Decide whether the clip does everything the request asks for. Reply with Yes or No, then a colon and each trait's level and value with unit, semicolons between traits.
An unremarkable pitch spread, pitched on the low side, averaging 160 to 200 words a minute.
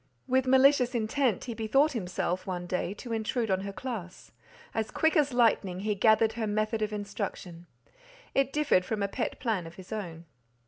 No: average, 4.6 semitones; high, 220 Hz; average, 180 wpm